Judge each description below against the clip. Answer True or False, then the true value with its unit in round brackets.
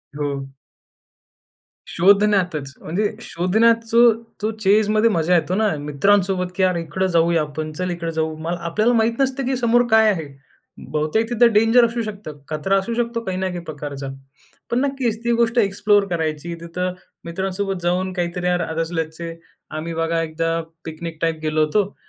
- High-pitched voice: False (180 Hz)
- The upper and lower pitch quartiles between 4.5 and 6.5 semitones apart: True (5.0 semitones)